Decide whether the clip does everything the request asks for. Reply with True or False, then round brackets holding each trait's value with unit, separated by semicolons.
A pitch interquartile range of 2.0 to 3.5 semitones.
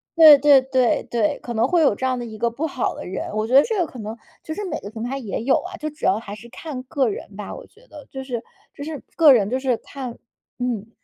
False (4.5 semitones)